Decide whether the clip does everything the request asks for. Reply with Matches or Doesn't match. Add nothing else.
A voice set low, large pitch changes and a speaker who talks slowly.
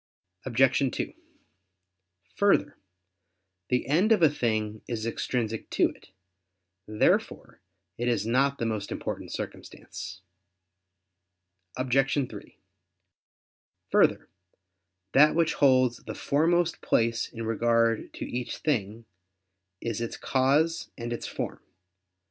Doesn't match